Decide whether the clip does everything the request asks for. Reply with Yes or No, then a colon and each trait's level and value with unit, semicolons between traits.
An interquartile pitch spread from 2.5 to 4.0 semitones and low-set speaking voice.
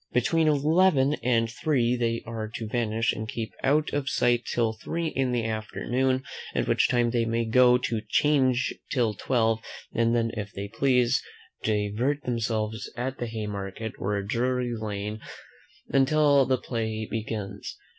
Yes: average, 2.8 semitones; low, 120 Hz